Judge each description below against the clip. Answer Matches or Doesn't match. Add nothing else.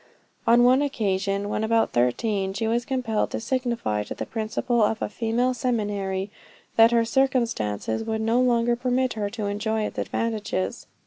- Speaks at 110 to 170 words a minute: Matches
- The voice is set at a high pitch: Matches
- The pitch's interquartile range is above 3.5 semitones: Doesn't match